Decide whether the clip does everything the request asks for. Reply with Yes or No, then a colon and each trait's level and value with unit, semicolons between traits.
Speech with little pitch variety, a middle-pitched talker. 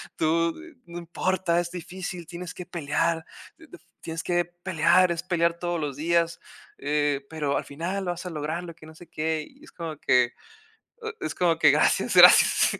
Yes: narrow, 1.9 semitones; medium, 170 Hz